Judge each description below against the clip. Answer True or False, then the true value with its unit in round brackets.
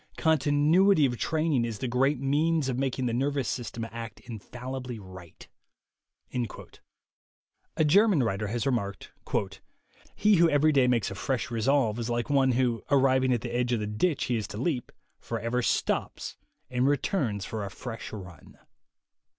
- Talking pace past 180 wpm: False (160 wpm)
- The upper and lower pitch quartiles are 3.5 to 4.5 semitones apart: True (3.8 semitones)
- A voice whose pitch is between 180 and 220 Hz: False (125 Hz)